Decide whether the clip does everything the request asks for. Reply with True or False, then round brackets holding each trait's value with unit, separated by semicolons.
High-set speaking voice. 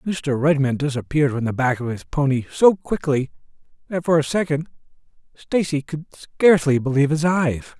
False (145 Hz)